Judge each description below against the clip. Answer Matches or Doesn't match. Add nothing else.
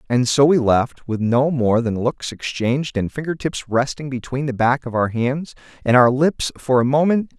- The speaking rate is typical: Doesn't match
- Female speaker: Doesn't match